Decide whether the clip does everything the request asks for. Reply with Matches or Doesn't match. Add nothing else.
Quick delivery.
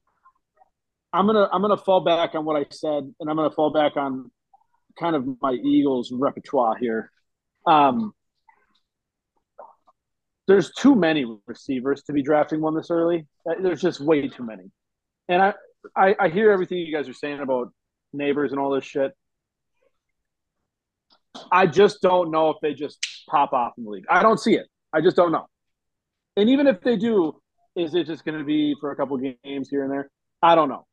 Doesn't match